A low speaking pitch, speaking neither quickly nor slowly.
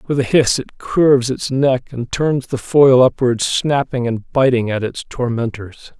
Yes: low, 125 Hz; average, 180 wpm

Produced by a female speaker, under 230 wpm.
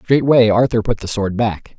No: male; average, 200 wpm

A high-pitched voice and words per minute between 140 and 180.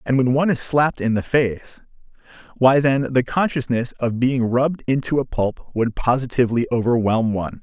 No: low, 125 Hz; average, 165 wpm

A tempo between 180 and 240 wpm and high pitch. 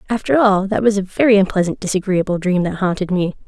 Yes: fast, 205 wpm; high, 195 Hz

